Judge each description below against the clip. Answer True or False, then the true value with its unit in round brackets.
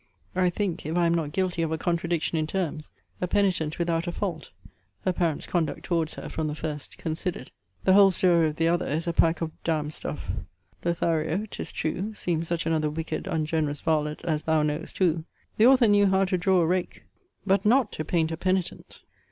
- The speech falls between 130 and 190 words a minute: False (205 wpm)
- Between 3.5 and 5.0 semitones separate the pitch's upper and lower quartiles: False (2.6 semitones)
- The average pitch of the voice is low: False (170 Hz)